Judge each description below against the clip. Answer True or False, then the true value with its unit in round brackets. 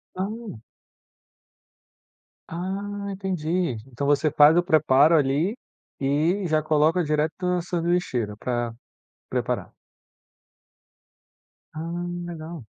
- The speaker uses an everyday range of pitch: True (3.6 semitones)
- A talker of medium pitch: True (160 Hz)